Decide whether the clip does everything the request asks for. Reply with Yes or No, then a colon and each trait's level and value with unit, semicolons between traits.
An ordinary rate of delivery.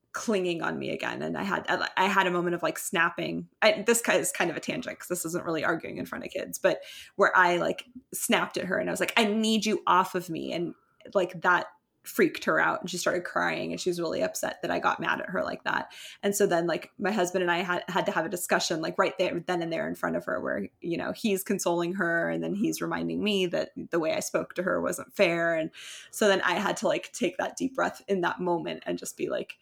No: fast, 270 wpm